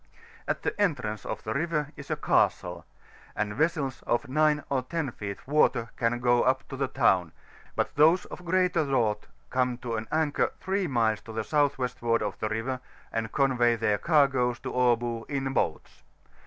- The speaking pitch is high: No, low, 130 Hz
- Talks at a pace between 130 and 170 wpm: No, average, 180 wpm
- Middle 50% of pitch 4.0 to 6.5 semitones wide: Yes, average, 4.3 semitones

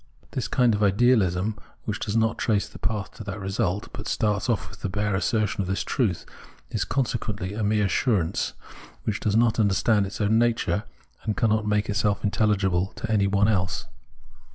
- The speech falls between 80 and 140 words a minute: No, average, 180 wpm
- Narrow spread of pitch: Yes, narrow, 2.1 semitones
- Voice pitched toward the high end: No, low, 105 Hz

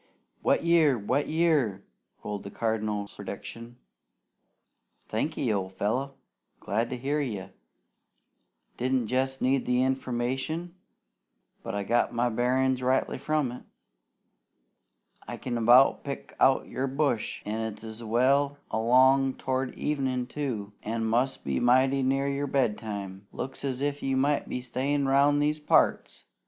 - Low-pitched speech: Yes, low, 130 Hz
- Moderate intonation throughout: Yes, average, 3.4 semitones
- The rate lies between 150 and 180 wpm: No, slow, 135 wpm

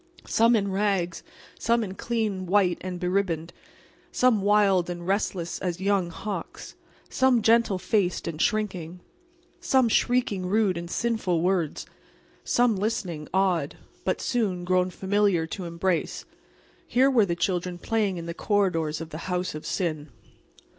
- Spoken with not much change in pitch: No, average, 3.5 semitones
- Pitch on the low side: No, high, 190 Hz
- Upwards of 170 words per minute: No, average, 140 wpm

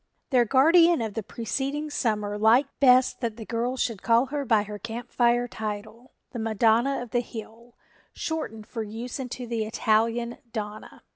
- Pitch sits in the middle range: No, high, 235 Hz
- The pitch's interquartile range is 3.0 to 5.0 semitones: No, narrow, 2.4 semitones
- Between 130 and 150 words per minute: No, average, 165 wpm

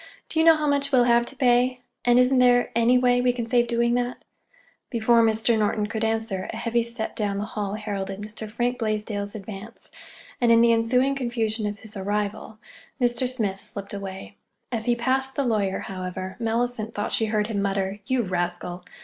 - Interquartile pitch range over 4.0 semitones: No, average, 2.9 semitones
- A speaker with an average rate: Yes, average, 190 wpm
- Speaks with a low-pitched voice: No, high, 225 Hz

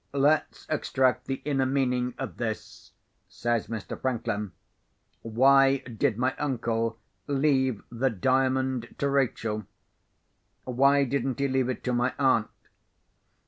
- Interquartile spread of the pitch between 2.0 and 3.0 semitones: Yes, narrow, 2.4 semitones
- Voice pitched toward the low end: Yes, low, 130 Hz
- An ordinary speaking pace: No, slow, 120 wpm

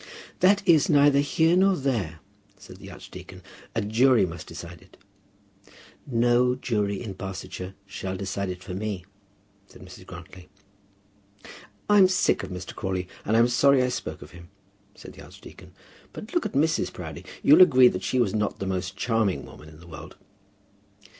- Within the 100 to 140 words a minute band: No, average, 165 wpm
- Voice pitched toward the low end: Yes, low, 105 Hz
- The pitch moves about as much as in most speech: No, wide, 6.4 semitones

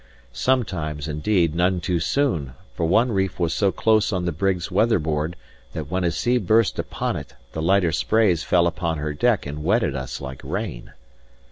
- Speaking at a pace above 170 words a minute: Yes, average, 180 wpm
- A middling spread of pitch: Yes, average, 4.5 semitones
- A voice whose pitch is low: Yes, very low, 90 Hz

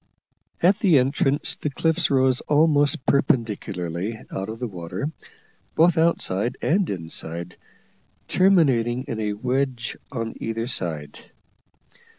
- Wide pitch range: Yes, wide, 6.3 semitones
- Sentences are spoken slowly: Yes, slow, 115 wpm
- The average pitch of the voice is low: Yes, low, 125 Hz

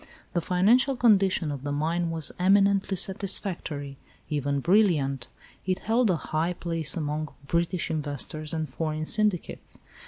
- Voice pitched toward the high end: No, medium, 165 Hz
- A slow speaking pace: Yes, slow, 130 wpm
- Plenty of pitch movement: No, average, 4.3 semitones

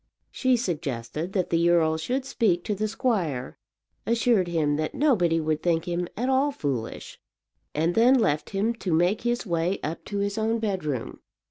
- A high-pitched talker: No, medium, 180 Hz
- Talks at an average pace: Yes, average, 170 wpm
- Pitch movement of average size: No, wide, 5.9 semitones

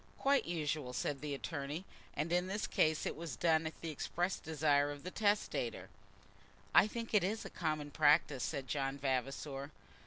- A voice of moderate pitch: Yes, medium, 155 Hz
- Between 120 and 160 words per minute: No, average, 175 wpm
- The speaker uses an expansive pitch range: No, average, 3.7 semitones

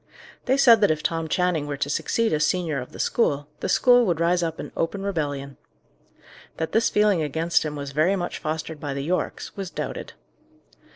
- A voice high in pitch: No, medium, 165 Hz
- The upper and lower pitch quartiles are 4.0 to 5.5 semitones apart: Yes, average, 4.4 semitones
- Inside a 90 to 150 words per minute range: No, average, 195 wpm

